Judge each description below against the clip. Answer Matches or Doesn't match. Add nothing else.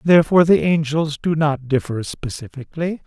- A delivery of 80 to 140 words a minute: Matches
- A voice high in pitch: Doesn't match